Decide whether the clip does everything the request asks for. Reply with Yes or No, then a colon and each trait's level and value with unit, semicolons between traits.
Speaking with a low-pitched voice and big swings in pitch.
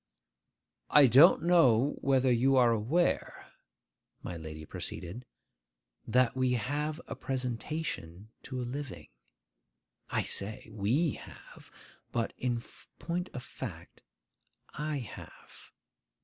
No: low, 125 Hz; average, 4.4 semitones